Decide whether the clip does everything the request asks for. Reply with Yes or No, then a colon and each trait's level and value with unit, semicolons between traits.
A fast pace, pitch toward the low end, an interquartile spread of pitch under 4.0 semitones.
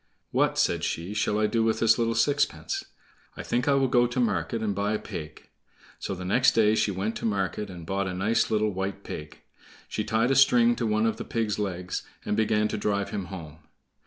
Yes: fast, 220 wpm; low, 105 Hz; average, 2.9 semitones